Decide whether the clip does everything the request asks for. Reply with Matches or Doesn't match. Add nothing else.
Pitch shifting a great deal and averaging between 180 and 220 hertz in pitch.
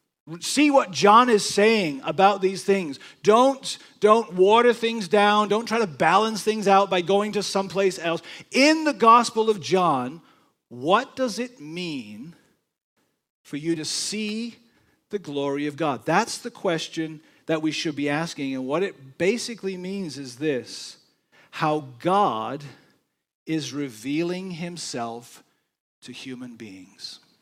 Matches